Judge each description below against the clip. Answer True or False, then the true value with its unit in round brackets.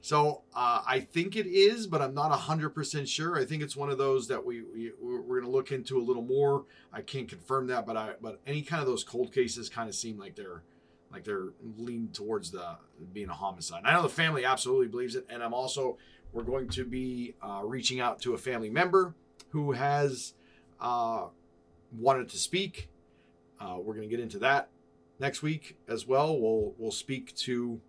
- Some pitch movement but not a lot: False (5.7 semitones)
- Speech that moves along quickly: True (210 wpm)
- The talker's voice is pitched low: True (130 Hz)